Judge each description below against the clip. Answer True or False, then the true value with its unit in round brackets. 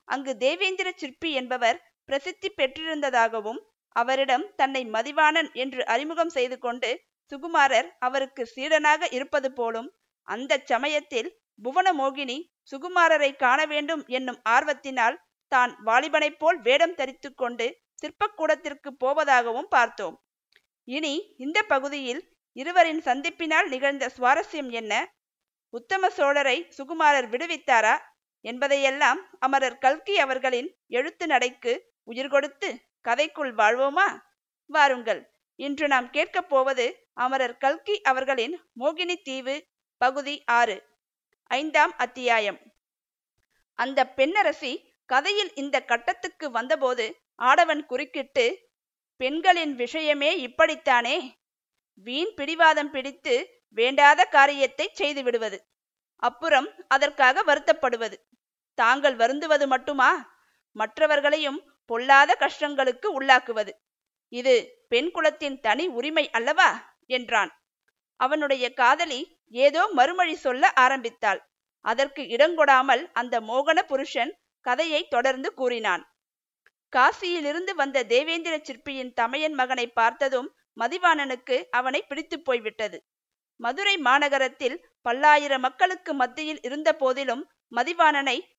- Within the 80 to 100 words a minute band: True (95 wpm)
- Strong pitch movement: False (4.2 semitones)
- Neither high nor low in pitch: False (280 Hz)